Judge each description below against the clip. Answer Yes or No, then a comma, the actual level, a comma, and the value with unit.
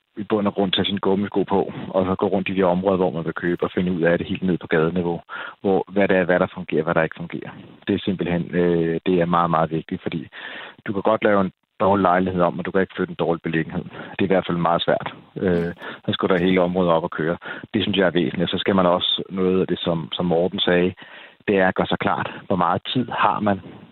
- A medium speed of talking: No, fast, 270 wpm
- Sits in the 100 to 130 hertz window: No, very low, 90 Hz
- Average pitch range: No, narrow, 2.1 semitones